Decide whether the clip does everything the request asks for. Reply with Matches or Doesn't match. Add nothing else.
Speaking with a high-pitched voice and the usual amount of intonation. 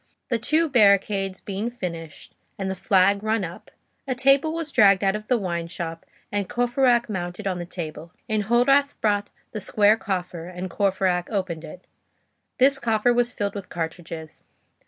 Matches